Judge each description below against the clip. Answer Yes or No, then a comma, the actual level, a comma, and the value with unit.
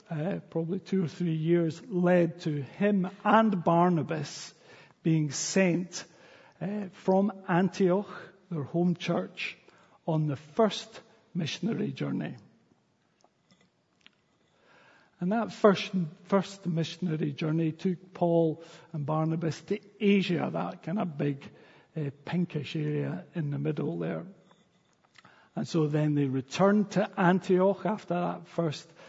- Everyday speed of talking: No, slow, 120 wpm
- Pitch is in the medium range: Yes, medium, 175 Hz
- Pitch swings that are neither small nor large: Yes, average, 3.1 semitones